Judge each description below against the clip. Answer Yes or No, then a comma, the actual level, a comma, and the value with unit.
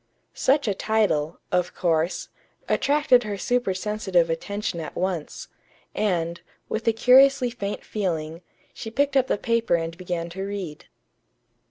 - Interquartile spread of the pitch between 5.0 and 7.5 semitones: Yes, wide, 5.4 semitones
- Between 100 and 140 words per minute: Yes, slow, 135 wpm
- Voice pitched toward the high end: Yes, high, 200 Hz